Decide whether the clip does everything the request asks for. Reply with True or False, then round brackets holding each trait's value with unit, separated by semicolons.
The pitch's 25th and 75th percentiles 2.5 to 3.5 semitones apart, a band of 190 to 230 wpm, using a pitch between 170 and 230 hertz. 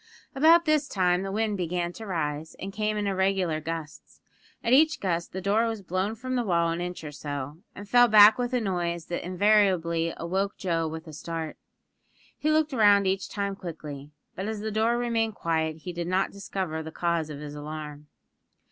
False (4.5 semitones; 195 wpm; 185 Hz)